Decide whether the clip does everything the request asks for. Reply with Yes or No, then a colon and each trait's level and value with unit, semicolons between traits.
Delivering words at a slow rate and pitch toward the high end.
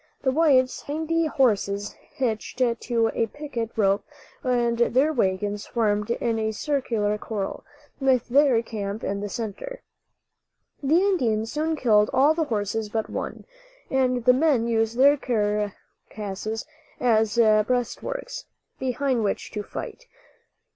Yes: slow, 130 wpm; high, 235 Hz